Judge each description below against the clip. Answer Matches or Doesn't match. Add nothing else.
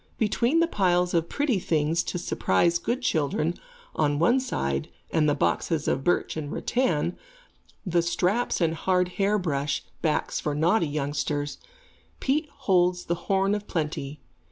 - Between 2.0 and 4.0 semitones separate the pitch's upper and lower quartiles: Doesn't match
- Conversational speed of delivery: Matches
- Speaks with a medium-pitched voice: Matches